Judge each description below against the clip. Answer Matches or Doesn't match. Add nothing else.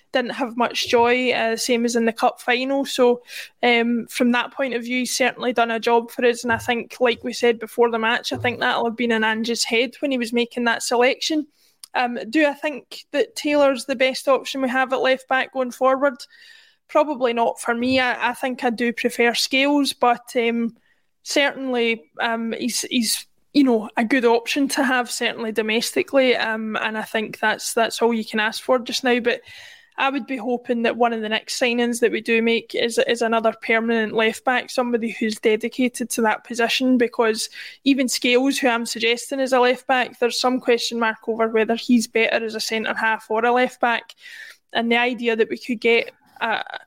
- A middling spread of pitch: Doesn't match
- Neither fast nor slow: Doesn't match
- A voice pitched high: Matches